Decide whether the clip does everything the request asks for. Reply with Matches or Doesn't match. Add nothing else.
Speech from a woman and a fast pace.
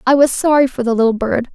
Matches